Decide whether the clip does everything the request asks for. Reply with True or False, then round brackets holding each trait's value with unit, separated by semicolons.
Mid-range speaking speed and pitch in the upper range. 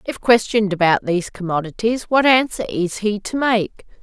True (165 wpm; 210 Hz)